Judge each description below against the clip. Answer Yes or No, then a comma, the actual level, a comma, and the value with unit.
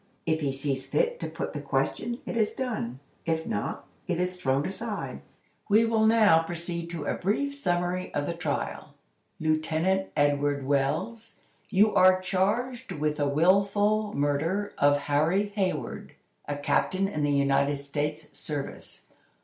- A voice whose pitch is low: No, medium, 170 Hz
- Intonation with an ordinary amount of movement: No, wide, 5.9 semitones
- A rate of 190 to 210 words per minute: No, average, 150 wpm